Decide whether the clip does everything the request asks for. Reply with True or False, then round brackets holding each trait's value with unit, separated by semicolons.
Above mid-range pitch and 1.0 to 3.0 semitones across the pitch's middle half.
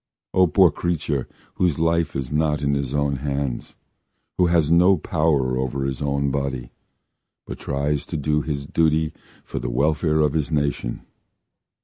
False (75 Hz; 2.4 semitones)